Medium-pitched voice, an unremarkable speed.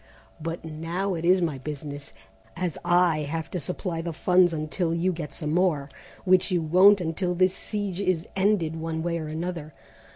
Yes: medium, 170 Hz; average, 175 wpm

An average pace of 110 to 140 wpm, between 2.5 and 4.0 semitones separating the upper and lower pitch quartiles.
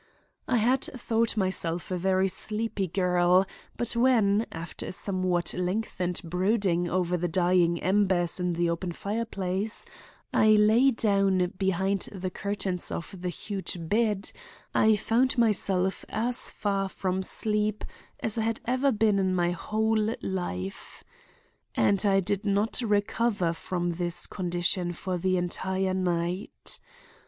Yes: slow, 135 wpm; average, 3.2 semitones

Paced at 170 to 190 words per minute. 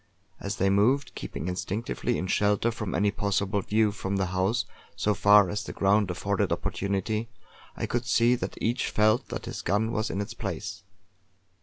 Yes: average, 175 wpm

